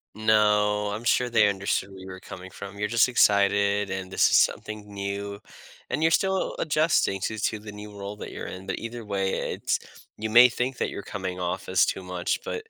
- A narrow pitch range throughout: Yes, narrow, 2.0 semitones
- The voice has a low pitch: Yes, low, 105 Hz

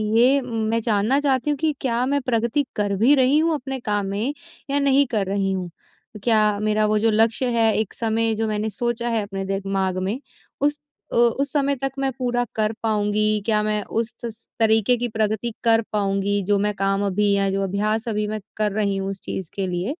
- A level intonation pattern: No, average, 3.1 semitones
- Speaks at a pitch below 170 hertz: No, high, 220 Hz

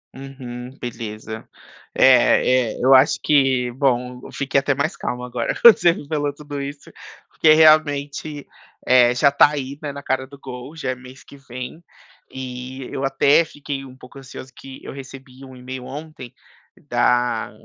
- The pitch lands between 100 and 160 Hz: Yes, low, 135 Hz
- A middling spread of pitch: No, narrow, 2.1 semitones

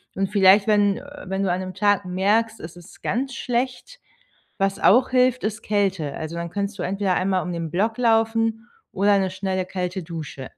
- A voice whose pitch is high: Yes, high, 195 Hz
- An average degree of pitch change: Yes, average, 3.3 semitones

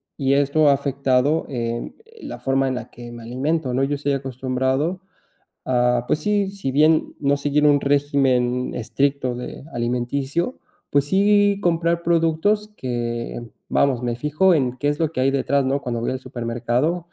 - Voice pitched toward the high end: No, medium, 140 Hz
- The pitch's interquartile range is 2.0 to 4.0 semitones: Yes, average, 3.7 semitones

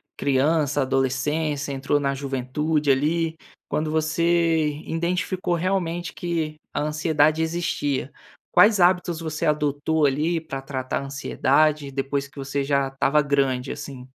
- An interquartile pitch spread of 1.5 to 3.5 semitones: Yes, average, 2.8 semitones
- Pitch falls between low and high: Yes, medium, 150 Hz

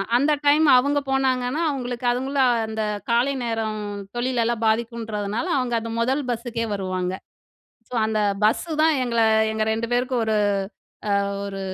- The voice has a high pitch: Yes, high, 235 Hz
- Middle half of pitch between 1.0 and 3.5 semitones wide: Yes, average, 2.9 semitones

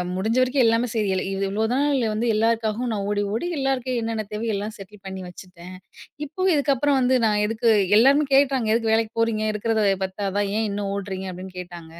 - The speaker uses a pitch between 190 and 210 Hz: No, high, 220 Hz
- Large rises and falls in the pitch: No, average, 3.8 semitones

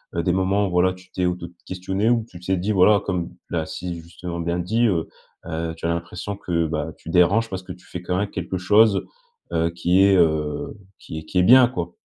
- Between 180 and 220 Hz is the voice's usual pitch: No, very low, 90 Hz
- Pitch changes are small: Yes, narrow, 2.3 semitones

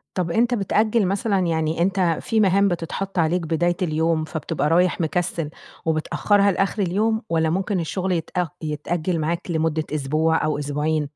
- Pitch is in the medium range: Yes, medium, 170 Hz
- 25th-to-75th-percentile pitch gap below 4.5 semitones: Yes, average, 3.4 semitones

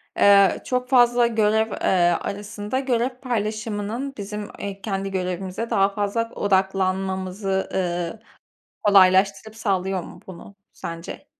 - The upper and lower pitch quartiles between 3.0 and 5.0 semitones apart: No, narrow, 2.6 semitones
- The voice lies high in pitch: Yes, high, 200 Hz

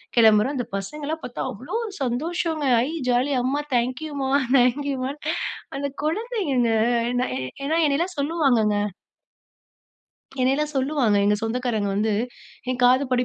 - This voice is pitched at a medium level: No, very high, 265 Hz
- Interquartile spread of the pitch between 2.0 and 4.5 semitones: Yes, average, 3.7 semitones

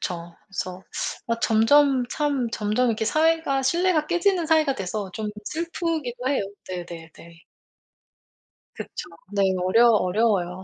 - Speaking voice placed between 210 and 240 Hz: Yes, high, 235 Hz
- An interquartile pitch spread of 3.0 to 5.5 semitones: No, wide, 7.9 semitones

